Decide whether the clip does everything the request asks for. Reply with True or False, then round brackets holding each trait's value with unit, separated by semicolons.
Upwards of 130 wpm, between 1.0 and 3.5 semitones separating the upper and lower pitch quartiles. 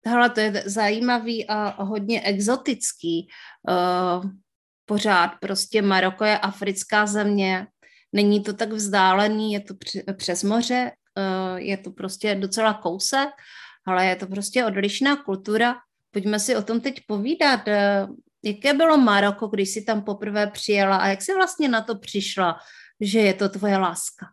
True (145 wpm; 2.5 semitones)